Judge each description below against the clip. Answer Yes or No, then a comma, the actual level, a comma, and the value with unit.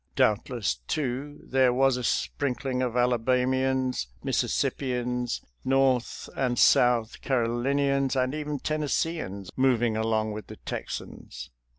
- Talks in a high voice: No, low, 125 Hz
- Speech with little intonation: Yes, narrow, 2.1 semitones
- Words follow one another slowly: Yes, slow, 115 wpm